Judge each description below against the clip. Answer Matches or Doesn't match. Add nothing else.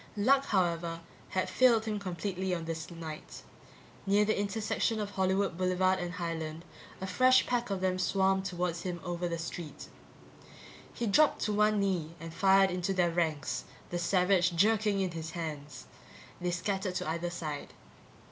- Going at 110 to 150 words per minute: Doesn't match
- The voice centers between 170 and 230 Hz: Matches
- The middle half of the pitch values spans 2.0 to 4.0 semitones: Matches